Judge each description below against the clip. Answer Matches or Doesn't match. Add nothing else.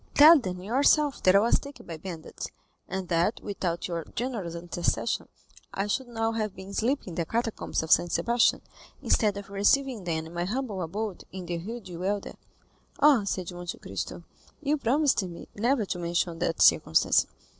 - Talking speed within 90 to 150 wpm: Doesn't match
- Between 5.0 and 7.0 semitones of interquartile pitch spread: Matches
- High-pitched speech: Matches